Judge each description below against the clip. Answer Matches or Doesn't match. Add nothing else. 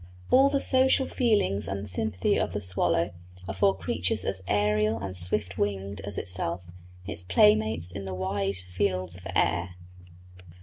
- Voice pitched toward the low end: Matches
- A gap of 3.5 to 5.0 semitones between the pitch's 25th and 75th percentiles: Doesn't match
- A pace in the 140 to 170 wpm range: Matches